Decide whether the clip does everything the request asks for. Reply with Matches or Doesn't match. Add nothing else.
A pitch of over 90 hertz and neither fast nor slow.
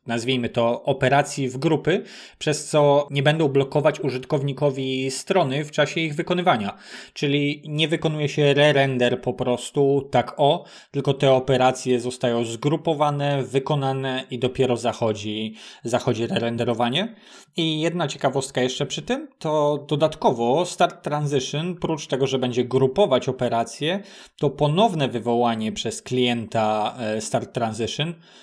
Matches